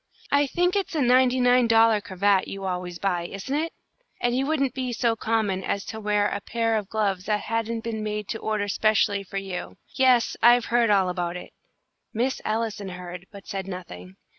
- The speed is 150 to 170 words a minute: No, average, 195 wpm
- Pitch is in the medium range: No, high, 215 Hz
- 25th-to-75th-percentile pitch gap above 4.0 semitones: No, average, 3.6 semitones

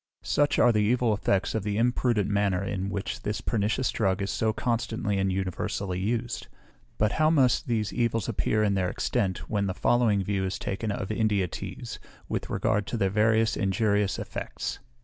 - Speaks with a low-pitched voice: Yes, low, 105 Hz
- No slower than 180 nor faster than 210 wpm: Yes, average, 185 wpm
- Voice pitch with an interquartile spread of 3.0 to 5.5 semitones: No, narrow, 2.6 semitones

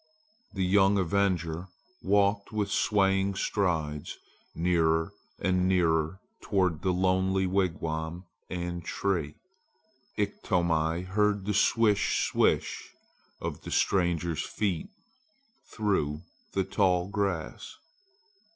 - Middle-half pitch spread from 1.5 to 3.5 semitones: Yes, average, 2.9 semitones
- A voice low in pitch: Yes, very low, 95 Hz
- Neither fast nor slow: No, slow, 95 wpm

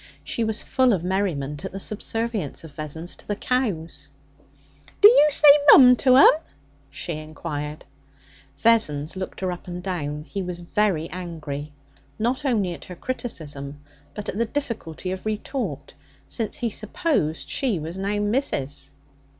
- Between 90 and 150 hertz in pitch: No, medium, 185 Hz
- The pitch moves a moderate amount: No, wide, 6.6 semitones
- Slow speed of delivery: No, average, 150 wpm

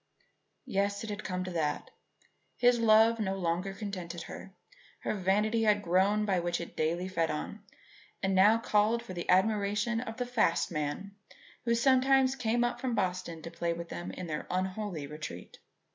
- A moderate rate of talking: Yes, average, 175 wpm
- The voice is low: No, high, 195 Hz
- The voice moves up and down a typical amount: Yes, average, 4.3 semitones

